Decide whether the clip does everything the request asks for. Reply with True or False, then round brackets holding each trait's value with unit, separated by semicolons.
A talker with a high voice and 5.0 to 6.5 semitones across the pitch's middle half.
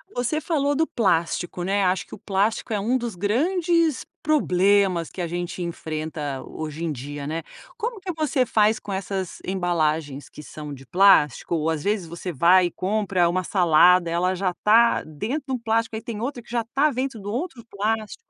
True (195 Hz; 5.6 semitones)